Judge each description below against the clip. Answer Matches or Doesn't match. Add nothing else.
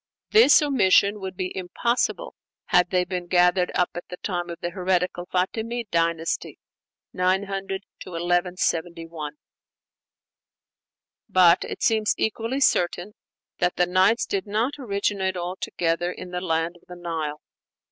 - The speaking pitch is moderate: Matches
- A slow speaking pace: Matches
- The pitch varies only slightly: Matches